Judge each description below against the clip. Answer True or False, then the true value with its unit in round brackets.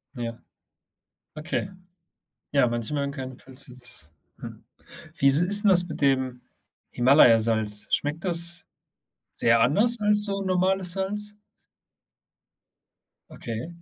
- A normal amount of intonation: False (7.3 semitones)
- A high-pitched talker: False (145 Hz)